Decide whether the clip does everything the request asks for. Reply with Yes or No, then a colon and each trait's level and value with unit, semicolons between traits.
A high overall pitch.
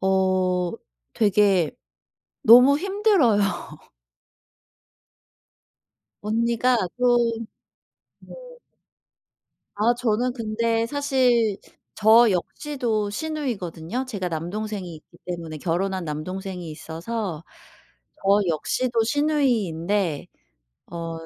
Yes: high, 210 Hz